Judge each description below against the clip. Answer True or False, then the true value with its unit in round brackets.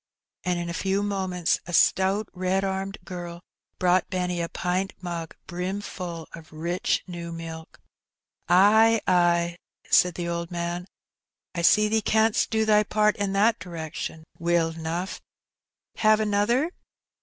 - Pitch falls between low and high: True (180 Hz)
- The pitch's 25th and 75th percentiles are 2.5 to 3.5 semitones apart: True (2.9 semitones)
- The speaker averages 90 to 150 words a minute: True (140 wpm)